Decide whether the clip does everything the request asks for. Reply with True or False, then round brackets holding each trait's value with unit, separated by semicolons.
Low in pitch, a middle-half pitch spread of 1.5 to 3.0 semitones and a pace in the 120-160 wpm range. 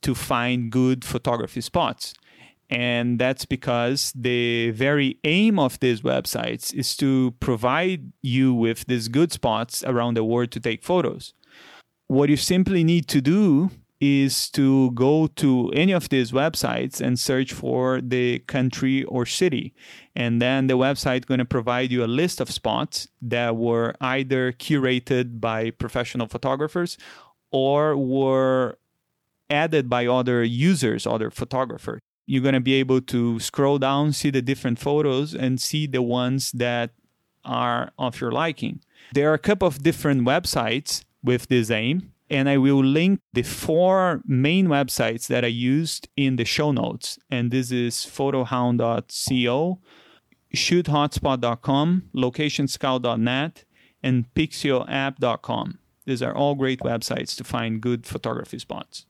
True (130 Hz; 2.7 semitones; 140 wpm)